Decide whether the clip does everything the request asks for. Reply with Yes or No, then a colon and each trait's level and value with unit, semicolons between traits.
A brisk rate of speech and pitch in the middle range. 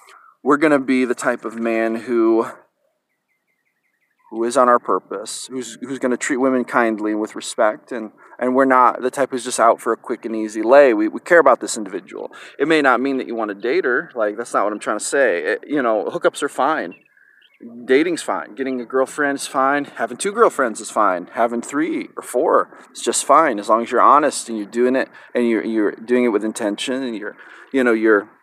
No: fast, 225 wpm; low, 125 Hz